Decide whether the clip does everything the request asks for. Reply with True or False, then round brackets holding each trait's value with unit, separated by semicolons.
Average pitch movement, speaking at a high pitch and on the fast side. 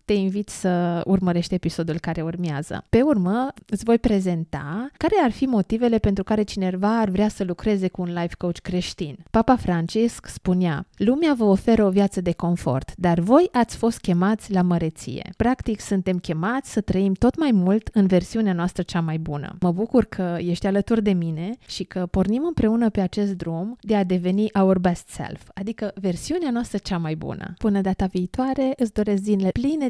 True (4.0 semitones; 195 Hz; 185 wpm)